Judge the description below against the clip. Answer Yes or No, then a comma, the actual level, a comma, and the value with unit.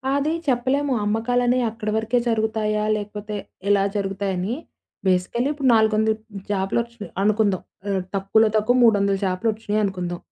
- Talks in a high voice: Yes, high, 215 Hz